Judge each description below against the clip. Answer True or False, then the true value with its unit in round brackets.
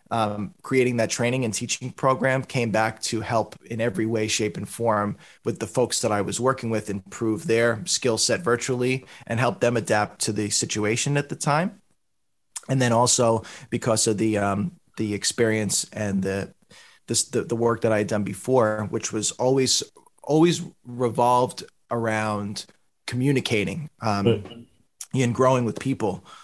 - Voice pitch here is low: True (115 Hz)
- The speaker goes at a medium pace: True (165 wpm)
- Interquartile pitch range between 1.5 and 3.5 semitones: True (3.0 semitones)